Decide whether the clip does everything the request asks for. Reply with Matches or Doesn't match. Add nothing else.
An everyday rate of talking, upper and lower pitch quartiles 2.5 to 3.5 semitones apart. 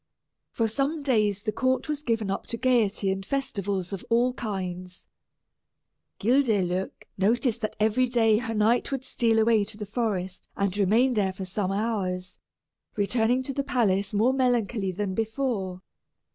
Doesn't match